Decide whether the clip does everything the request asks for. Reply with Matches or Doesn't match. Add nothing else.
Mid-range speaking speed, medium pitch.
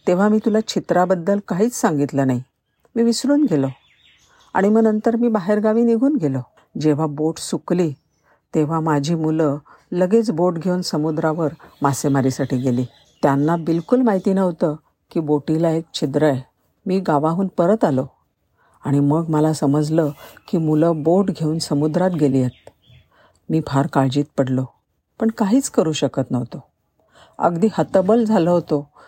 Doesn't match